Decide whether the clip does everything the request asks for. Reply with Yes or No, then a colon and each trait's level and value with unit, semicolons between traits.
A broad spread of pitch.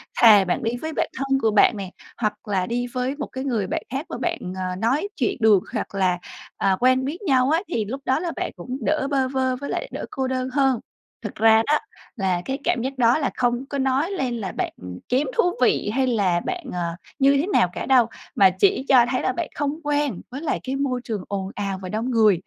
No: average, 4.7 semitones